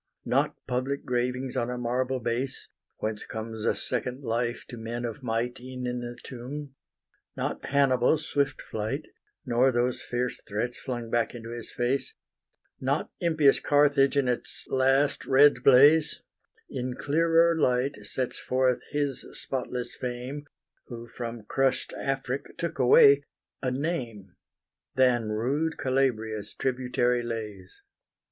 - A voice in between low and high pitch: No, low, 125 Hz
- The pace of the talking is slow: Yes, slow, 130 wpm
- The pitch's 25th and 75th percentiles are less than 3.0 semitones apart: Yes, narrow, 2.4 semitones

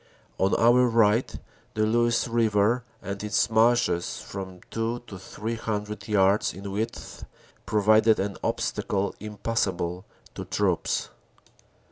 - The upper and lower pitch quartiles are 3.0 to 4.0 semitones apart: No, narrow, 2.5 semitones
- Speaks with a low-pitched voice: Yes, low, 105 Hz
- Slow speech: Yes, slow, 115 wpm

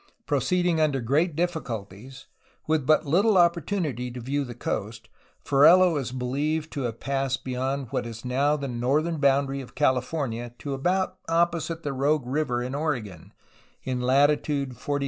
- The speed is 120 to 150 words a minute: No, average, 160 wpm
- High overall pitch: No, medium, 140 Hz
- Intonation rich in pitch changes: No, average, 3.8 semitones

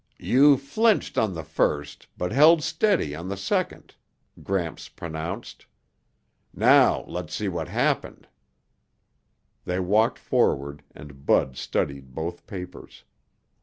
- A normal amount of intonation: No, wide, 6.6 semitones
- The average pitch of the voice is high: No, very low, 90 Hz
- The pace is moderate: No, slow, 115 wpm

